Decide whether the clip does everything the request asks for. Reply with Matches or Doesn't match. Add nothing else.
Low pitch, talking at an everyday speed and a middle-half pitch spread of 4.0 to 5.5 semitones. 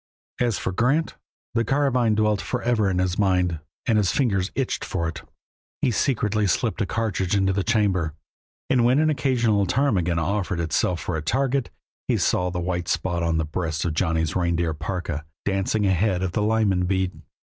Matches